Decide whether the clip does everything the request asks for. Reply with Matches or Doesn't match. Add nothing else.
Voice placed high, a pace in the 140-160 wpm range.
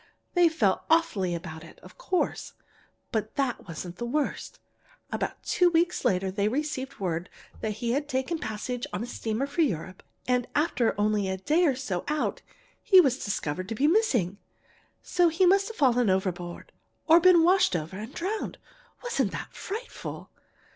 Doesn't match